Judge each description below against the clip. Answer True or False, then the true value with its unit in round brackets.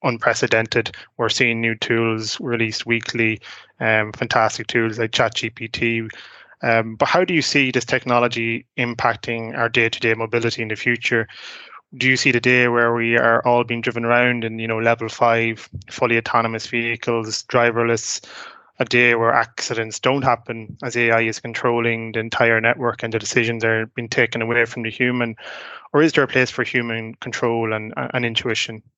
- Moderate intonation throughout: False (1.3 semitones)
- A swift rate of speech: False (170 wpm)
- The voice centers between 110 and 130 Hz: True (115 Hz)